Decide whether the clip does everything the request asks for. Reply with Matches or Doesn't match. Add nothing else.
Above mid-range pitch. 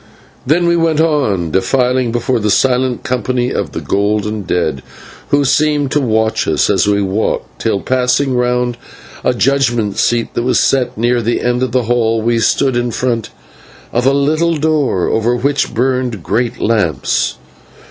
Doesn't match